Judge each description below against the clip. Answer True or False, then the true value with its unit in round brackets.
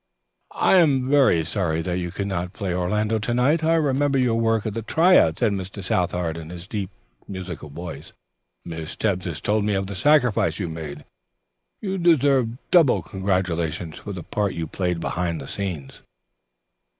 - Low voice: True (95 Hz)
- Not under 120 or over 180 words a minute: True (175 wpm)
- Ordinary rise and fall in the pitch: False (5.9 semitones)